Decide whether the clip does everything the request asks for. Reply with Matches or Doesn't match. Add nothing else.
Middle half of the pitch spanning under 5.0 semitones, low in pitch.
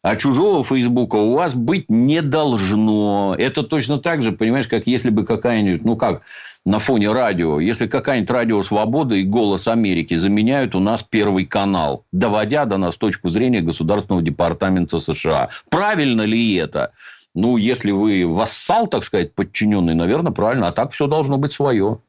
Doesn't match